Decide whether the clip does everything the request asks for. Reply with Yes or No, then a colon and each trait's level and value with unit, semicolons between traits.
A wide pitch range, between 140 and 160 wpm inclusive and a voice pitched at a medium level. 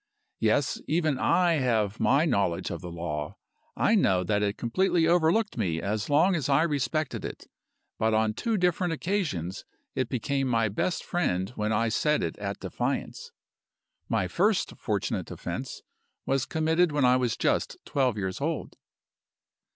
No: wide, 7.7 semitones; average, 155 wpm; low, 125 Hz